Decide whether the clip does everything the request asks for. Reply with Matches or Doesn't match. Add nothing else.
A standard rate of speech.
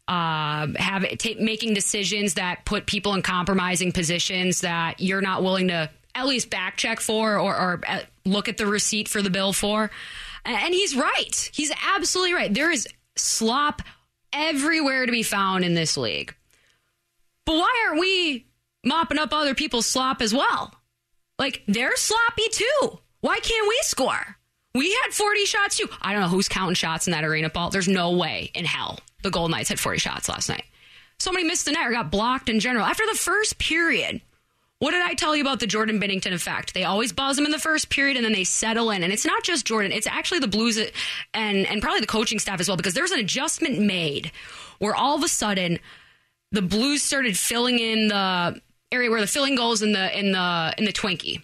Doesn't match